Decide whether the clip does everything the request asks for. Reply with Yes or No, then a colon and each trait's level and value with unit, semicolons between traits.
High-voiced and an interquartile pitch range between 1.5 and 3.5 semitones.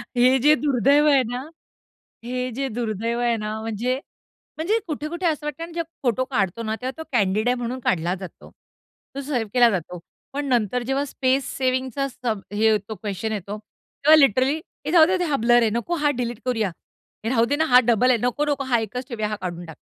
No: very high, 250 Hz; average, 4.2 semitones